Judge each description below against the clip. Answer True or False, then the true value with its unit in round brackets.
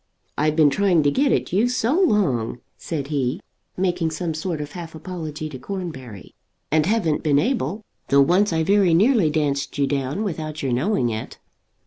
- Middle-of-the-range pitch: True (160 Hz)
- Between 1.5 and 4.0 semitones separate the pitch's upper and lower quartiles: False (5.1 semitones)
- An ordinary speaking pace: True (175 wpm)